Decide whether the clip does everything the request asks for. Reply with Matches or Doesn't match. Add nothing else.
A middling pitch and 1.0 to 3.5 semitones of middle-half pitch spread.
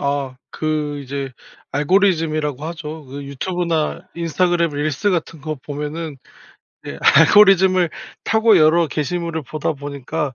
Matches